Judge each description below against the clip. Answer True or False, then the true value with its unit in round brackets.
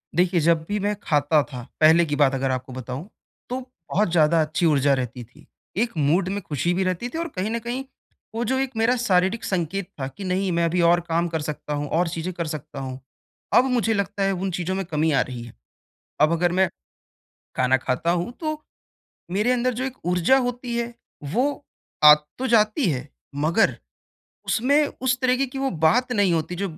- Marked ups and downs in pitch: True (7.2 semitones)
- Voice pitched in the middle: True (180 Hz)